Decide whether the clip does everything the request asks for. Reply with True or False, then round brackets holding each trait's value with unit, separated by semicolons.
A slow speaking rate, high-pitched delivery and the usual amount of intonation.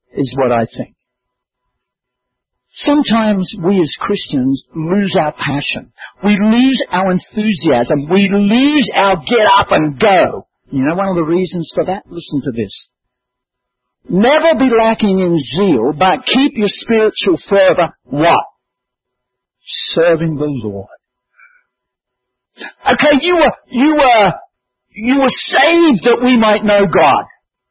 False (130 wpm; 195 Hz; 8.5 semitones)